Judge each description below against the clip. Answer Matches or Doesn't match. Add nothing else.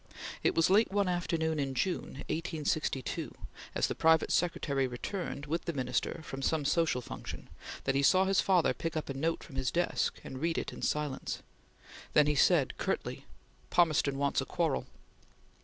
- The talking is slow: Doesn't match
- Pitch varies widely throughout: Doesn't match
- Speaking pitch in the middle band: Matches